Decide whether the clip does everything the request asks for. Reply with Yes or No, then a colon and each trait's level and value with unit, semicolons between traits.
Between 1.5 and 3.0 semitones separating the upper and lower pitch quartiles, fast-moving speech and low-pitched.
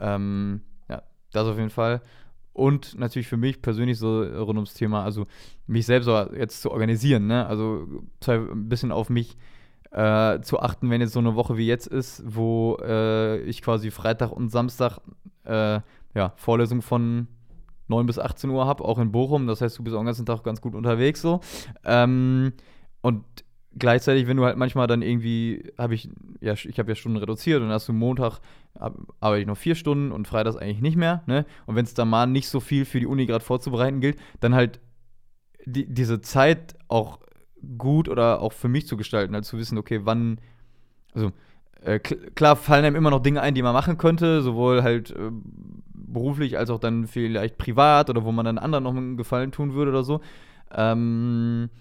Yes: narrow, 2.6 semitones; fast, 200 wpm; low, 120 Hz